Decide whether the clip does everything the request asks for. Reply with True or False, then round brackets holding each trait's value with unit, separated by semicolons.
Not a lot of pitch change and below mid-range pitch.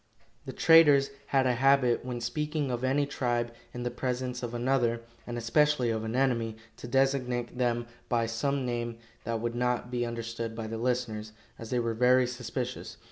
True (1.8 semitones; 120 Hz)